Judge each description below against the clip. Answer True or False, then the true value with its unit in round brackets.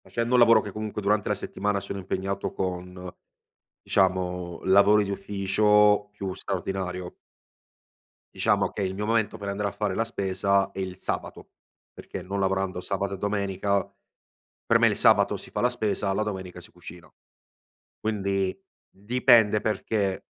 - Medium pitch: False (100 Hz)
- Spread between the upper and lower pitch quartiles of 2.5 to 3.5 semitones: False (1.8 semitones)